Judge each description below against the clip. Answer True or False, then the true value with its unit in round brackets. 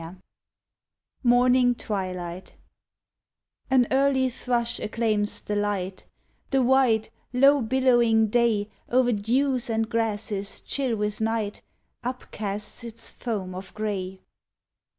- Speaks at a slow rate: True (110 wpm)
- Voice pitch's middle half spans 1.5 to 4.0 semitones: True (3.2 semitones)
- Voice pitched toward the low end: False (225 Hz)